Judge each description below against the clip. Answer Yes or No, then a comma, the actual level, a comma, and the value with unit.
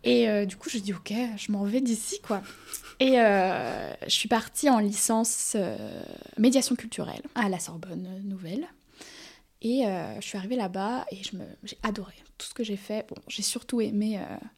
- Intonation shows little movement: No, average, 3.3 semitones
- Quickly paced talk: No, average, 200 wpm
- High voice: Yes, high, 215 Hz